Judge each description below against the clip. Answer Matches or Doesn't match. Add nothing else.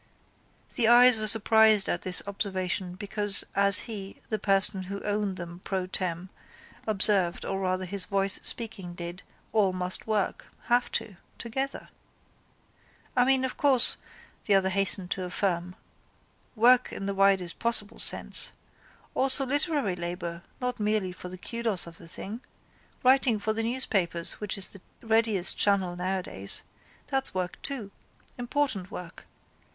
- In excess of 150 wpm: Doesn't match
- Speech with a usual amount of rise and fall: Matches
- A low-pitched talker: Doesn't match